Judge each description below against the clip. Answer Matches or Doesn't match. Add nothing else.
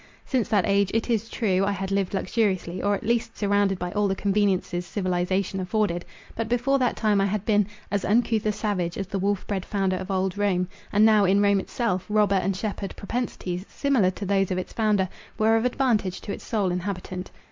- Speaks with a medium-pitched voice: Doesn't match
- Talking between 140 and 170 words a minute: Doesn't match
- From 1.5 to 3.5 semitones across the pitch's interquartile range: Matches